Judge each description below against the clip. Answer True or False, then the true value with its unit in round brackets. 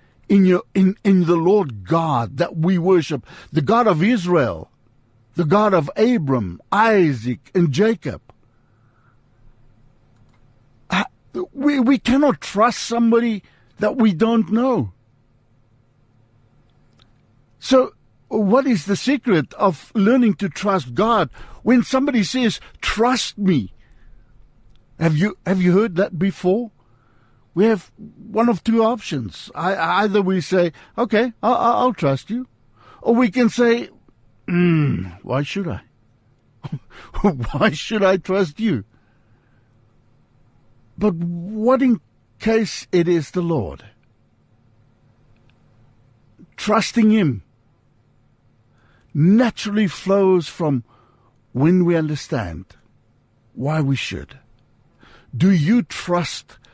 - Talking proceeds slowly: True (110 wpm)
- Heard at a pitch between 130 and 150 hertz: False (170 Hz)